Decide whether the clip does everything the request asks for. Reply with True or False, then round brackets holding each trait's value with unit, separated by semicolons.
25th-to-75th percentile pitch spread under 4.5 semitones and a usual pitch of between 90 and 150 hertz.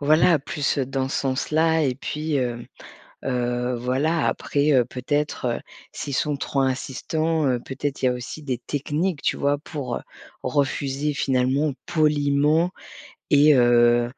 True (3.0 semitones; 140 Hz)